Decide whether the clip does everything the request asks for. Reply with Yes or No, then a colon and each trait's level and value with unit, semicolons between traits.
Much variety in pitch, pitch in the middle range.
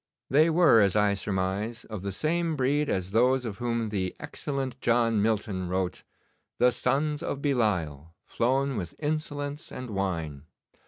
No: wide, 6.2 semitones; low, 115 Hz